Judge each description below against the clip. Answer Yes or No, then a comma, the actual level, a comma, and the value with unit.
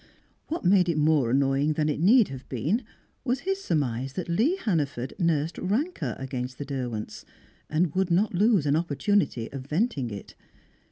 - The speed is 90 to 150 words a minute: No, average, 165 wpm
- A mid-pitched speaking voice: Yes, medium, 155 Hz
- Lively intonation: Yes, wide, 6.4 semitones